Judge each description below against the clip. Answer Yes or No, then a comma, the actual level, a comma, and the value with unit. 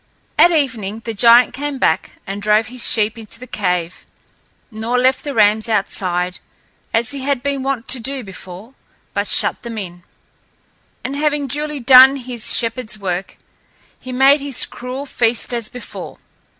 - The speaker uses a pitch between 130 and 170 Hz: No, high, 235 Hz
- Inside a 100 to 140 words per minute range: No, average, 160 wpm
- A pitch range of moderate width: Yes, average, 4.0 semitones